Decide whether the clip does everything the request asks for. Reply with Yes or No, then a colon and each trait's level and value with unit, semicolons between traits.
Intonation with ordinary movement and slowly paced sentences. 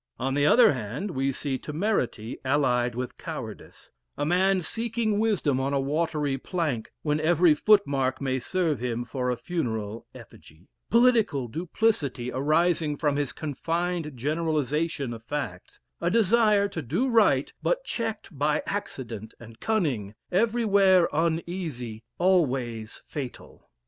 No: wide, 6.2 semitones; slow, 130 wpm